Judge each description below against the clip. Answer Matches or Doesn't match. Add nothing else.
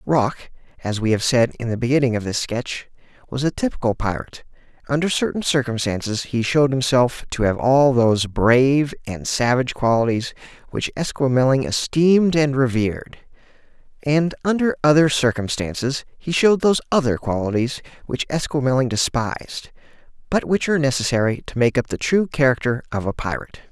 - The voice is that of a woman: Doesn't match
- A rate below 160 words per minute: Matches